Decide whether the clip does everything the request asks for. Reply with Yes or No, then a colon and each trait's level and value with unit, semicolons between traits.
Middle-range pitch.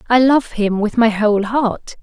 No: high, 225 Hz